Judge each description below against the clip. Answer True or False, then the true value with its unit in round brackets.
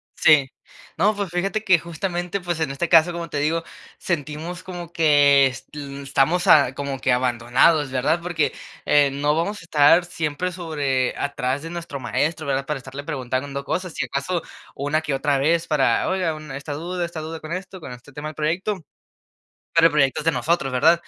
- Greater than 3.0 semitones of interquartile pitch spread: True (3.6 semitones)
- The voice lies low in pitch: False (155 Hz)